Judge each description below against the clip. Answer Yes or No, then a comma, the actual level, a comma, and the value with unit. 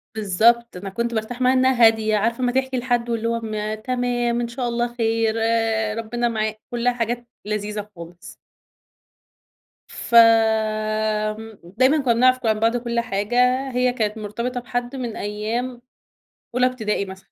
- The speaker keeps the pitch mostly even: Yes, narrow, 2.2 semitones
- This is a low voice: No, high, 230 Hz